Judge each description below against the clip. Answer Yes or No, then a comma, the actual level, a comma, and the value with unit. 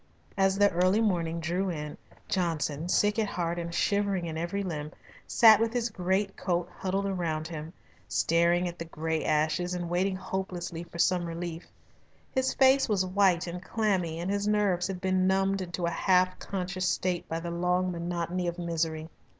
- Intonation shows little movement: Yes, narrow, 2.3 semitones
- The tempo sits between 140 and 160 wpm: No, average, 175 wpm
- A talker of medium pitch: Yes, medium, 180 Hz